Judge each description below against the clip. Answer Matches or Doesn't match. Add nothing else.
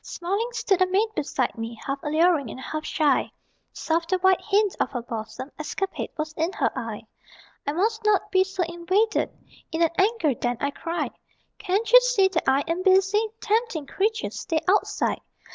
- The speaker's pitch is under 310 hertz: Doesn't match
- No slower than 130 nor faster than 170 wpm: Doesn't match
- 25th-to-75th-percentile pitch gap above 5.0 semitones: Matches